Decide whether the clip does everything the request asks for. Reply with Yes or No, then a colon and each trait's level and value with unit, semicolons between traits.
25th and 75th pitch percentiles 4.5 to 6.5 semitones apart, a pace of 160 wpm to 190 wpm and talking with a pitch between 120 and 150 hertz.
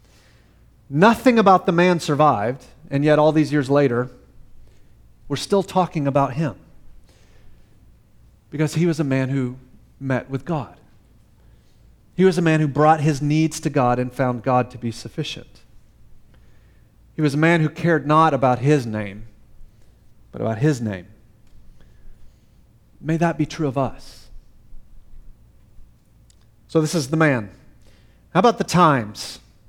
No: average, 5.2 semitones; average, 140 wpm; medium, 140 Hz